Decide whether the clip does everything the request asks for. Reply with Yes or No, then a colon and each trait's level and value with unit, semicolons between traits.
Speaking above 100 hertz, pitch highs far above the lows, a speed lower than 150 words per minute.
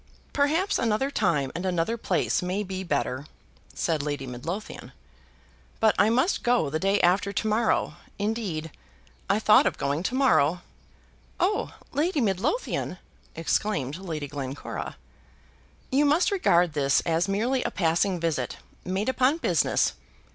Yes: high, 190 Hz; wide, 6.7 semitones; slow, 135 wpm